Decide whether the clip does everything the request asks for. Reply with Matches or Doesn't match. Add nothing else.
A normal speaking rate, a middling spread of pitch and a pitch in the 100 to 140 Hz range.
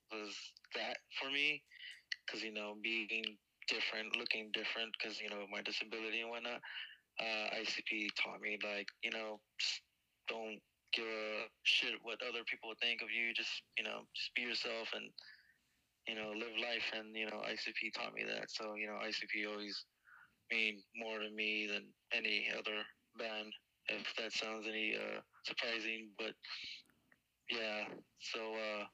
Doesn't match